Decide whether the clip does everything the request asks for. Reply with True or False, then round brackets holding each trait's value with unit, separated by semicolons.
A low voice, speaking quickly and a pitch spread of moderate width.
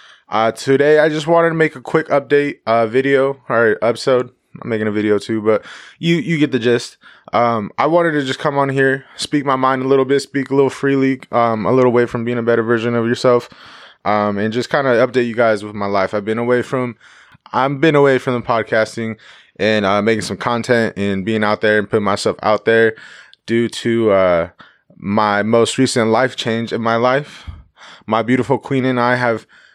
True (120 Hz; 215 wpm; 3.4 semitones)